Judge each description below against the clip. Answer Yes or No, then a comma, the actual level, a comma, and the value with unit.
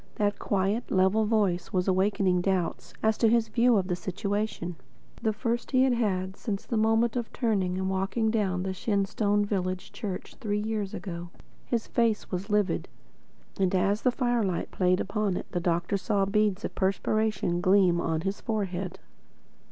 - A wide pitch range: No, average, 2.8 semitones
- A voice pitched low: No, high, 200 Hz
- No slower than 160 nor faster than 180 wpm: Yes, average, 165 wpm